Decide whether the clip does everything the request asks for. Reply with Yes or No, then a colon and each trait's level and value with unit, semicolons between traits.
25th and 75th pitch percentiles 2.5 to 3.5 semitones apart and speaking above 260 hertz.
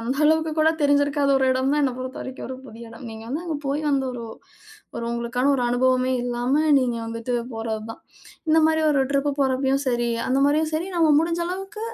No: average, 3.9 semitones; very high, 270 Hz